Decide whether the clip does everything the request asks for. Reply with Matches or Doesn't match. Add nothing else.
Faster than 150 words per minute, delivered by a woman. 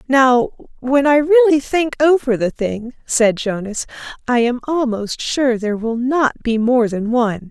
Matches